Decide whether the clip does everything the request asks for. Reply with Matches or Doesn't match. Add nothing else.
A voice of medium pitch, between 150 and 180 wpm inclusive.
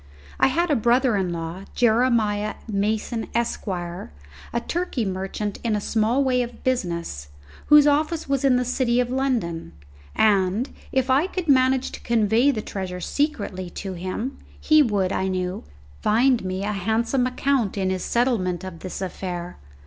Doesn't match